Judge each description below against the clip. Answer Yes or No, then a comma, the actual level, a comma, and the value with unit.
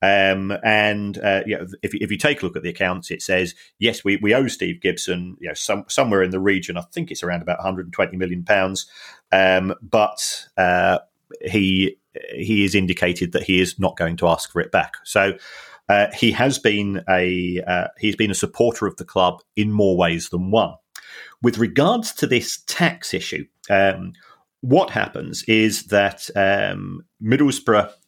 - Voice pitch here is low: Yes, low, 100 Hz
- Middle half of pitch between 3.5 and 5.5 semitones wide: No, narrow, 2.5 semitones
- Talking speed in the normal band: Yes, average, 185 wpm